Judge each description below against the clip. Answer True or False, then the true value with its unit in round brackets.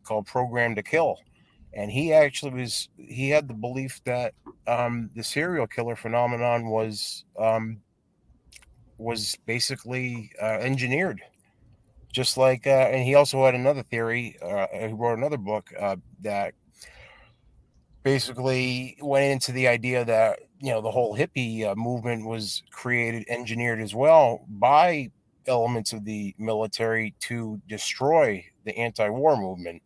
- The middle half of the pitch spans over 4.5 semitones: False (2.8 semitones)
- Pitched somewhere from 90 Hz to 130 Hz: True (120 Hz)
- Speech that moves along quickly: False (135 wpm)